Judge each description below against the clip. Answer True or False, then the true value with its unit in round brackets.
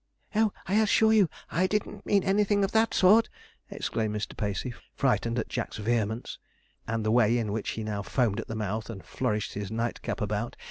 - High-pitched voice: False (115 Hz)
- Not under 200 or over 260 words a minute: False (190 wpm)